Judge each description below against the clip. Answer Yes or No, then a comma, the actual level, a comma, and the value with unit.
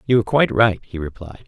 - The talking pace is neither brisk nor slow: No, fast, 245 wpm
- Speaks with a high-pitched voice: No, low, 105 Hz